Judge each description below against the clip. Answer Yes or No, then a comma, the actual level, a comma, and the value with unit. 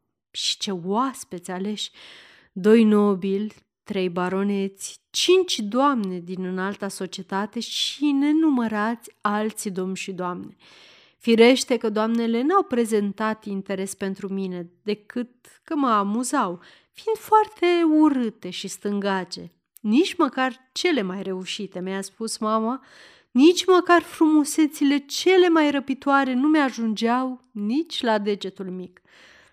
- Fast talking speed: No, slow, 115 wpm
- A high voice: Yes, high, 220 Hz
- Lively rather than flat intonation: Yes, wide, 6.1 semitones